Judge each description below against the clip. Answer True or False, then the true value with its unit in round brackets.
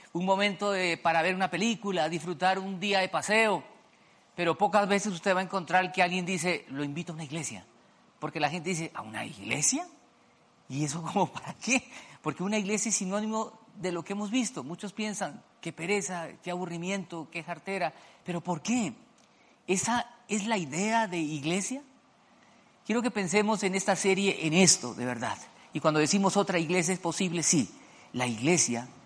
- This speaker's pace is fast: False (180 wpm)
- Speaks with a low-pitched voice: False (190 Hz)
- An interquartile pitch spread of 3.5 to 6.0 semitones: True (4.0 semitones)